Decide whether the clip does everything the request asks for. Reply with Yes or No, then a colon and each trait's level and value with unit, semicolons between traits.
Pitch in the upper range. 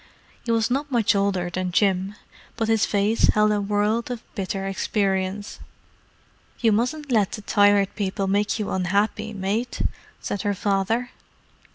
Yes: high, 205 Hz